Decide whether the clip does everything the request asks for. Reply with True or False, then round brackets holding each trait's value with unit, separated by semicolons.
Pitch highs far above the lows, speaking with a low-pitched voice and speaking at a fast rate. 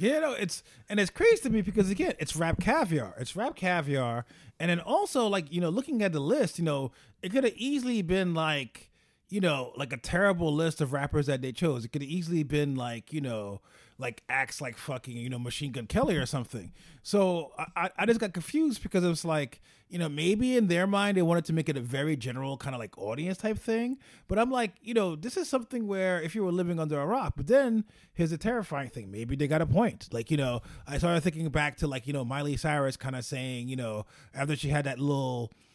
False (6.6 semitones; 155 Hz; 240 wpm)